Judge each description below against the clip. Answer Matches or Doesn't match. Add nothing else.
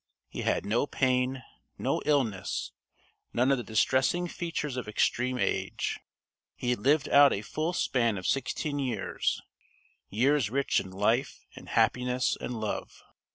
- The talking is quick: Doesn't match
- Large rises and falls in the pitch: Doesn't match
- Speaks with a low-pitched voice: Matches